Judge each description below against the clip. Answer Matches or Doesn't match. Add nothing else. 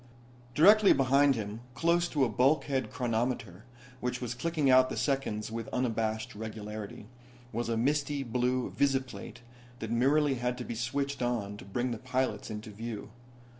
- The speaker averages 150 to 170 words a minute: Matches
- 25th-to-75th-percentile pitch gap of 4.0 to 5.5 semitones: Doesn't match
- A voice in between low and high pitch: Doesn't match